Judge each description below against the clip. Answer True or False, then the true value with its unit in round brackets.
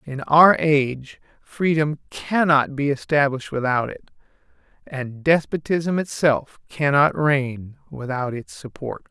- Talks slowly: True (110 wpm)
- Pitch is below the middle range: False (145 Hz)